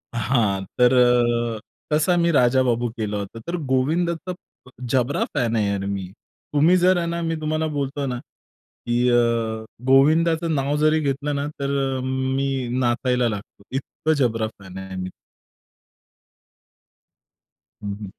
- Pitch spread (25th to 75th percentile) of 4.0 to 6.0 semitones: Yes, average, 4.6 semitones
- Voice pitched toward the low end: Yes, low, 130 Hz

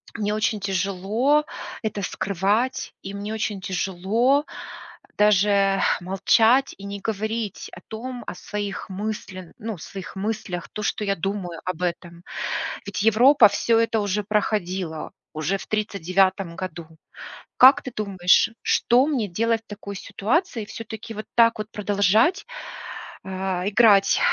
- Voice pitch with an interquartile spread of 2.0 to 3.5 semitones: Yes, narrow, 2.6 semitones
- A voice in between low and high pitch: No, high, 205 Hz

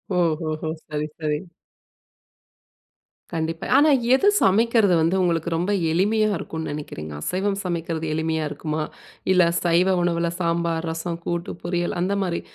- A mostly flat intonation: Yes, narrow, 2.2 semitones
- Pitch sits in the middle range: Yes, medium, 170 Hz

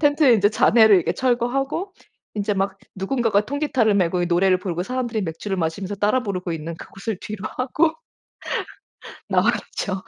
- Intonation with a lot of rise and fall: No, average, 5.0 semitones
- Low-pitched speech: No, high, 205 Hz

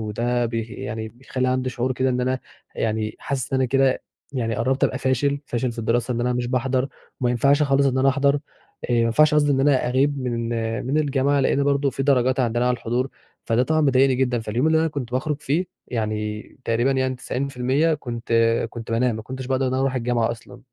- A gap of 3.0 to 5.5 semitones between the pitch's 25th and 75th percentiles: No, narrow, 2.4 semitones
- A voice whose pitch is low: Yes, low, 130 Hz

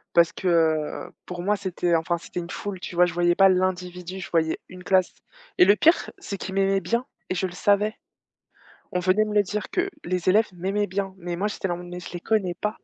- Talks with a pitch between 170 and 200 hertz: Yes, medium, 185 Hz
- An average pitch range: No, narrow, 2.2 semitones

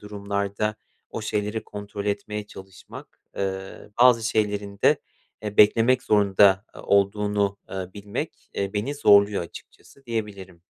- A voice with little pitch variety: Yes, narrow, 1.1 semitones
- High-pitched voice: No, low, 105 Hz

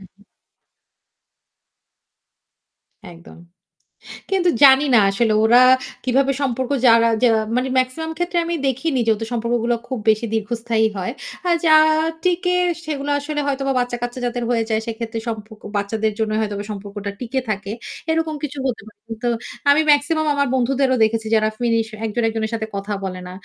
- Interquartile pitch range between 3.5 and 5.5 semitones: Yes, average, 3.8 semitones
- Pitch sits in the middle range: No, high, 235 Hz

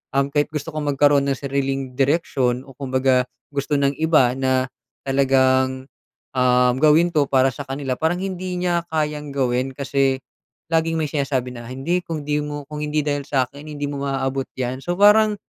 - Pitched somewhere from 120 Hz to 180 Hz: Yes, medium, 140 Hz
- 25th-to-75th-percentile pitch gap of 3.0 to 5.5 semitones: No, narrow, 2.5 semitones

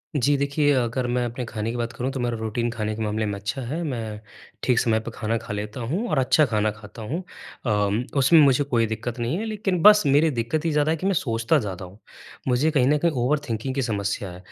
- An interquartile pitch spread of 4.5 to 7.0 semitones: Yes, average, 4.8 semitones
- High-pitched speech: No, low, 120 Hz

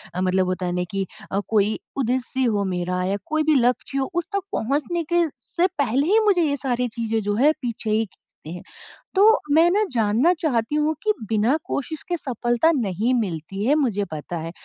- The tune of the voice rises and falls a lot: Yes, wide, 6.8 semitones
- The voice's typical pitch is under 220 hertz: No, high, 240 Hz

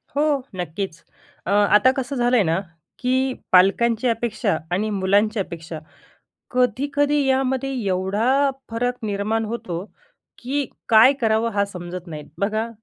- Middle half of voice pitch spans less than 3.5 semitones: No, average, 4.7 semitones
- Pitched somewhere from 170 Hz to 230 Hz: Yes, high, 220 Hz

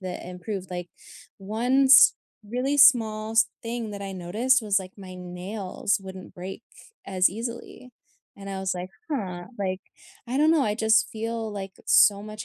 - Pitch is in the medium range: No, high, 205 Hz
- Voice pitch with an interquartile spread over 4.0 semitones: No, average, 3.6 semitones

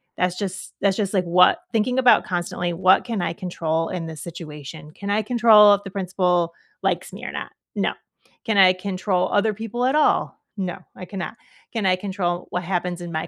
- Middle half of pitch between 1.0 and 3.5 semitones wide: Yes, average, 2.7 semitones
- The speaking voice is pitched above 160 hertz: Yes, medium, 185 Hz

